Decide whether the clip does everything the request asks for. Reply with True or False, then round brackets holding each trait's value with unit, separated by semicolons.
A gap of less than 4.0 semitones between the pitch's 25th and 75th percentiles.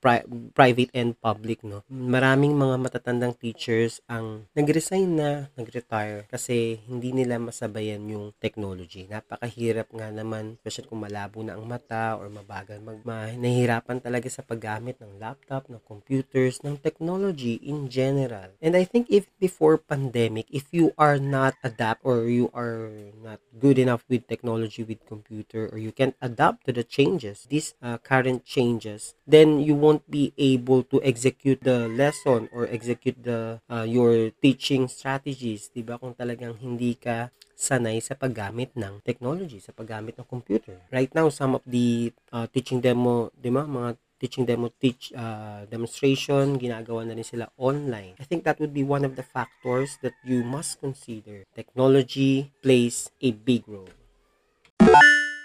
True (2.9 semitones)